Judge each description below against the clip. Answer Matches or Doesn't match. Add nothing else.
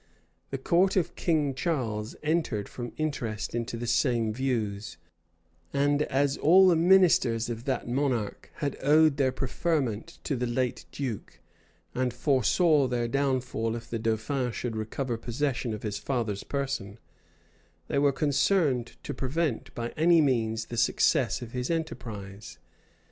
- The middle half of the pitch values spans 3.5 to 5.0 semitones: Matches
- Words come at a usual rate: Matches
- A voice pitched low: Matches